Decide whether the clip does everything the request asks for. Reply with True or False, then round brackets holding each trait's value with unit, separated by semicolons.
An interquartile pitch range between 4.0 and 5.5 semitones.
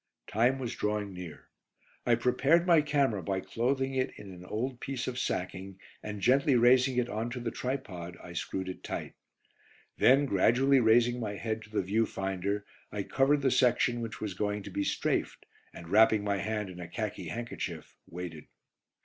True (4.5 semitones)